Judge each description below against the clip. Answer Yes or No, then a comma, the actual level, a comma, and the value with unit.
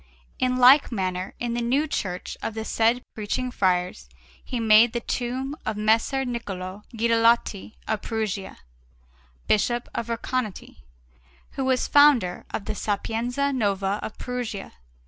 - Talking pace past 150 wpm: No, slow, 135 wpm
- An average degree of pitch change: Yes, average, 3.3 semitones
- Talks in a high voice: Yes, high, 230 Hz